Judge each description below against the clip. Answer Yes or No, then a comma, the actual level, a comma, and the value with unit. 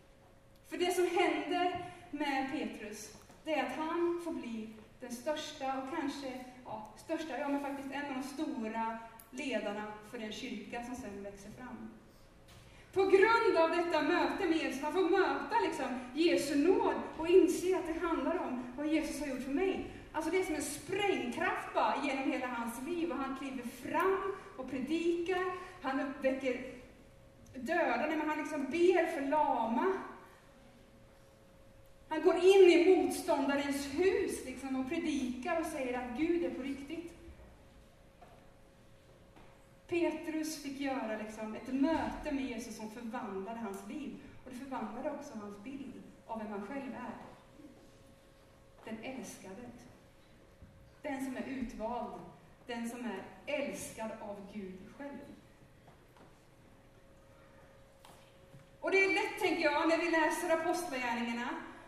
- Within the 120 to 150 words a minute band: Yes, average, 140 wpm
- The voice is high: Yes, very high, 285 Hz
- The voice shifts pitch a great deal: No, average, 5.0 semitones